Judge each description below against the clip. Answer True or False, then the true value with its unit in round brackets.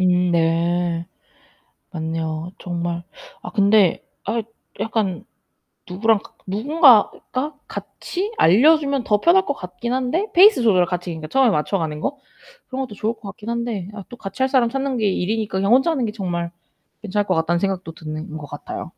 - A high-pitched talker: True (200 Hz)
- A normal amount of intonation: False (6.1 semitones)